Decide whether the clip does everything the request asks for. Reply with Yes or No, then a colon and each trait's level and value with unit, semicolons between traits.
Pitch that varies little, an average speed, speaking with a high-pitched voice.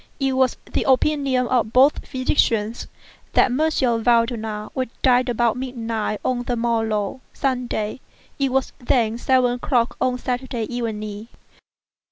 No: narrow, 2.3 semitones; slow, 130 wpm; high, 245 Hz